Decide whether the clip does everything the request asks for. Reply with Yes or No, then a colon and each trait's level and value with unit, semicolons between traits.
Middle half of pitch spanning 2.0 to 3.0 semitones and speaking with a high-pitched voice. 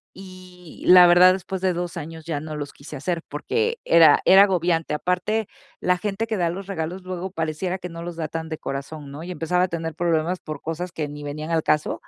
No: narrow, 2.6 semitones; medium, 170 Hz